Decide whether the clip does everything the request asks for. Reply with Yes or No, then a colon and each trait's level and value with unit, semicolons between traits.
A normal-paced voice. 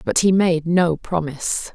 Yes: average, 170 wpm